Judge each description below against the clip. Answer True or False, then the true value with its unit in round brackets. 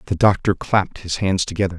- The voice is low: True (95 Hz)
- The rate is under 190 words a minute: False (200 wpm)